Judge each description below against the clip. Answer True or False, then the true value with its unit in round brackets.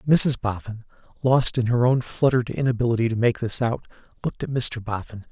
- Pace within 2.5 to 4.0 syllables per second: False (5.8 syllables/s)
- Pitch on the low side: True (120 Hz)